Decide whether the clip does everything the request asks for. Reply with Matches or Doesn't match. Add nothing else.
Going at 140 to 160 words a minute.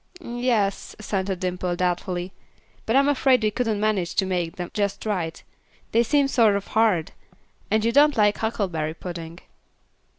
Matches